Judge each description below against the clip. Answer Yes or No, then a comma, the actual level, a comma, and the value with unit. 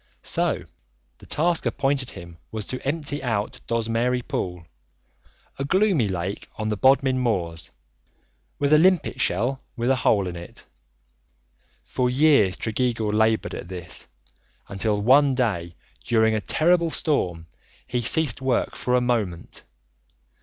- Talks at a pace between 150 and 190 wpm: No, slow, 135 wpm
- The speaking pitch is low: Yes, low, 120 Hz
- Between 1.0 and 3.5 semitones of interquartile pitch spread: No, average, 5.1 semitones